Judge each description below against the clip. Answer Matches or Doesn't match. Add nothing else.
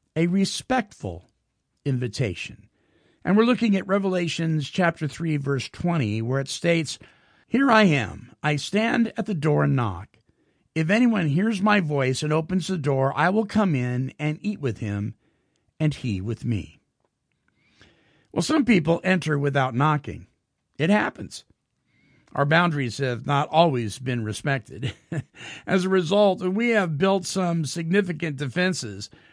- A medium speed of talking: Matches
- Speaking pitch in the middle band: Matches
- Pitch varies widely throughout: Matches